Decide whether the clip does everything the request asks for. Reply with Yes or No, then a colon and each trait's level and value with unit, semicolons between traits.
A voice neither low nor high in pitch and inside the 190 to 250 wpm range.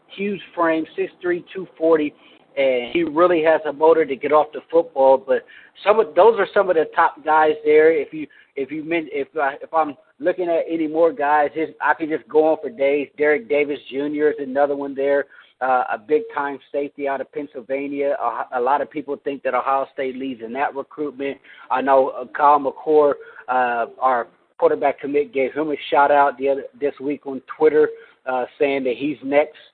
Yes: medium, 145 Hz; fast, 205 wpm